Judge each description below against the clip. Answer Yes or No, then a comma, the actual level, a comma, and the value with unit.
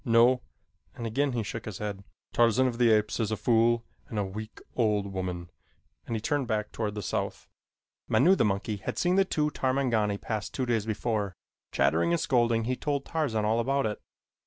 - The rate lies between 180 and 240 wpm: Yes, average, 195 wpm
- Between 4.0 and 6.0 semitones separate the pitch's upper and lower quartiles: No, average, 3.2 semitones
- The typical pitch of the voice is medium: No, low, 115 Hz